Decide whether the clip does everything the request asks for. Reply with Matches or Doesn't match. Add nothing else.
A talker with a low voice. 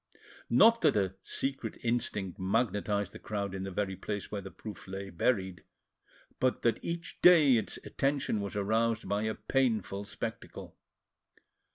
Matches